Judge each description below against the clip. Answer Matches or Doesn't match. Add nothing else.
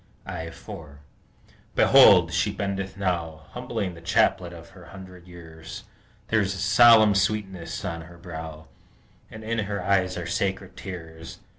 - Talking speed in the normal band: Matches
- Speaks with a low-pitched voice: Matches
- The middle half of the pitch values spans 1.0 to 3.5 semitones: Matches